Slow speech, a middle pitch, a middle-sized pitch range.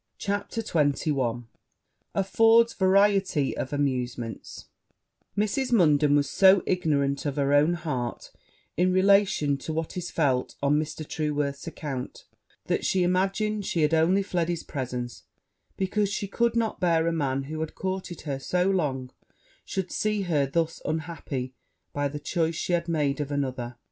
No: average, 150 wpm; medium, 160 Hz; average, 5.0 semitones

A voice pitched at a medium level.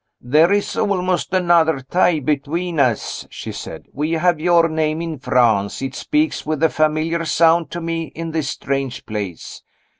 Yes: medium, 160 Hz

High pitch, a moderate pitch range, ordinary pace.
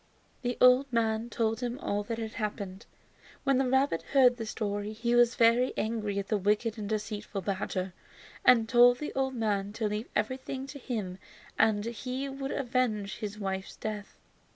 Yes: high, 225 Hz; average, 3.3 semitones; average, 175 wpm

